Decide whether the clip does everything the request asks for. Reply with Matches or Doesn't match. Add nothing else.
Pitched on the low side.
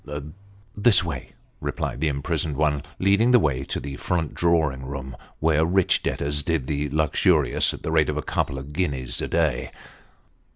Matches